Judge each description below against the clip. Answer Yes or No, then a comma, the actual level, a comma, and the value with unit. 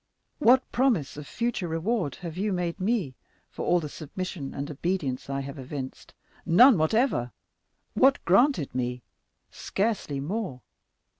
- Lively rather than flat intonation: Yes, wide, 7.7 semitones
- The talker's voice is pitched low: No, medium, 170 Hz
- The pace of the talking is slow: Yes, slow, 125 wpm